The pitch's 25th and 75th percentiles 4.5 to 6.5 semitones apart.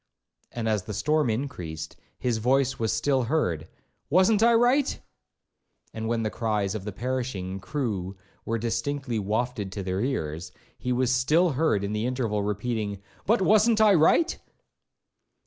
Yes: wide, 5.6 semitones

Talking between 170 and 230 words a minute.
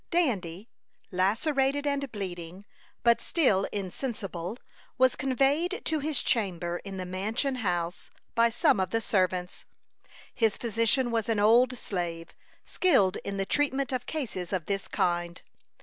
No: slow, 135 wpm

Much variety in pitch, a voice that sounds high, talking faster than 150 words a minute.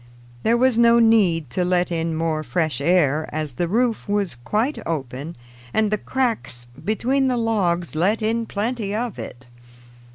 Yes: wide, 6.2 semitones; high, 195 Hz; average, 160 wpm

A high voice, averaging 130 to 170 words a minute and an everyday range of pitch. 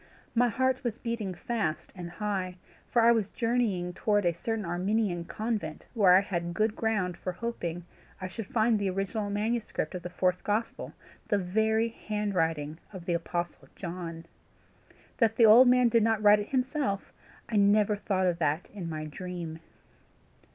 Yes: high, 205 Hz; average, 165 wpm; average, 4.0 semitones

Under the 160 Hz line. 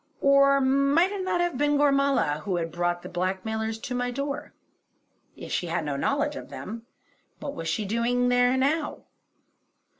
No: high, 245 Hz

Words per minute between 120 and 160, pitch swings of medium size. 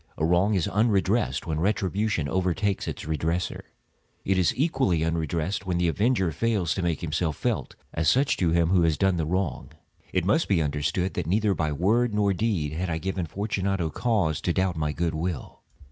No: average, 190 wpm; average, 3.6 semitones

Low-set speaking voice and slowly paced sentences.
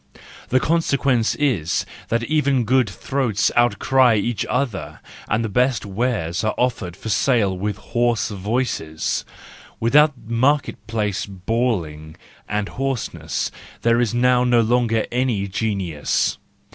Yes: low, 115 Hz; slow, 120 wpm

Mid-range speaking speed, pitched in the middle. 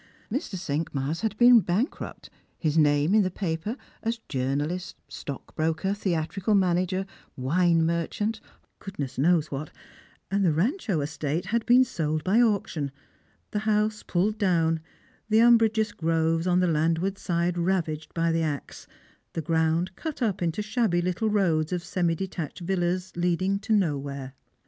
Yes: average, 150 wpm; medium, 175 Hz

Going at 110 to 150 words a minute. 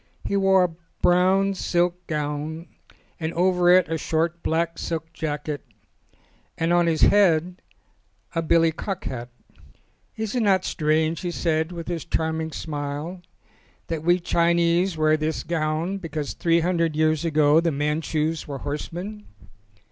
Yes: average, 145 wpm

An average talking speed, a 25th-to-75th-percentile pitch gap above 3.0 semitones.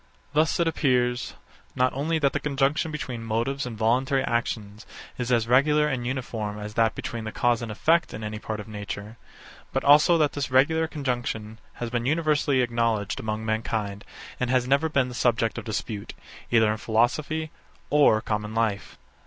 Yes: average, 175 wpm; average, 4.2 semitones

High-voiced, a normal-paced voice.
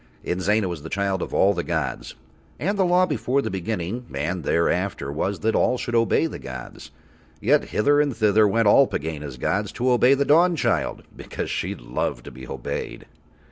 No: low, 105 Hz; average, 180 wpm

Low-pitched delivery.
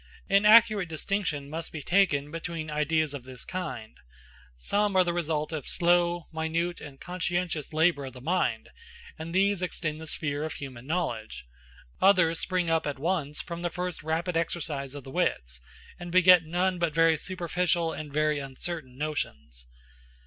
No: medium, 160 Hz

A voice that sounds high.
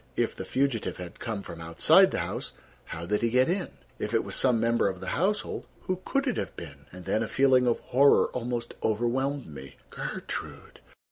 No: low, 115 Hz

